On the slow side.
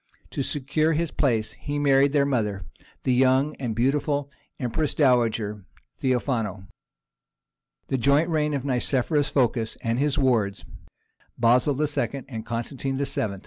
Yes: slow, 130 wpm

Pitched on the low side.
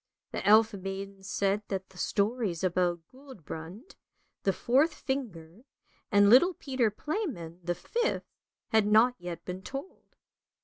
No: high, 205 Hz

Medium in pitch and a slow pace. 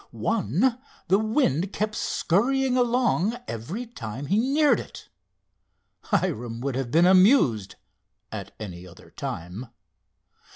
Yes: medium, 180 Hz; slow, 115 wpm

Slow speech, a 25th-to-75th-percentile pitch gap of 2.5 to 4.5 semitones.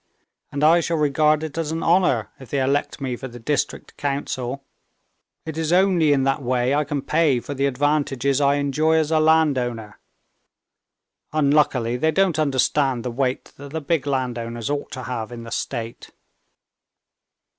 No: average, 165 wpm; average, 3.3 semitones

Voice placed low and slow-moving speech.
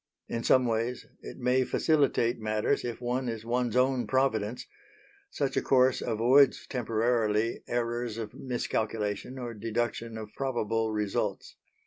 Yes: low, 120 Hz; slow, 130 wpm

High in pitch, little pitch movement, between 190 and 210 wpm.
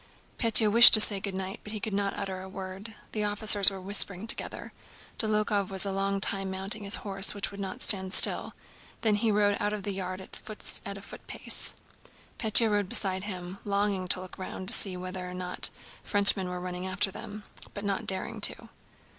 Yes: high, 200 Hz; narrow, 1.7 semitones; average, 195 wpm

